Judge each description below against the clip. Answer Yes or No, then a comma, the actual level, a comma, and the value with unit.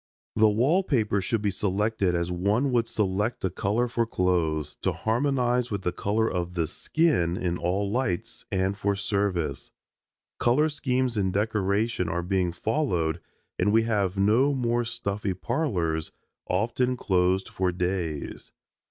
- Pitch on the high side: No, low, 100 Hz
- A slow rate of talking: No, average, 145 wpm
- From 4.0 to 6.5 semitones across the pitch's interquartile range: Yes, average, 4.5 semitones